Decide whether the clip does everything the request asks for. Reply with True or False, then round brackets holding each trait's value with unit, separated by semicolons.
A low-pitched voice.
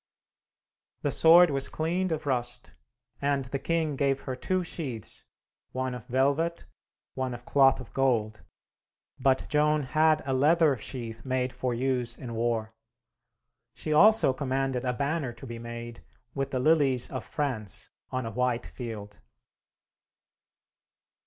True (130 Hz)